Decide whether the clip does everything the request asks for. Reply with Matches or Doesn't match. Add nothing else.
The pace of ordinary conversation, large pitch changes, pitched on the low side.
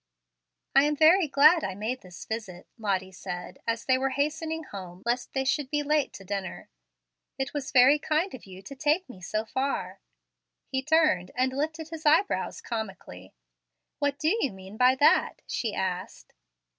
Doesn't match